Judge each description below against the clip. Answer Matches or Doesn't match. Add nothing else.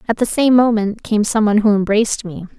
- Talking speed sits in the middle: Doesn't match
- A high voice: Matches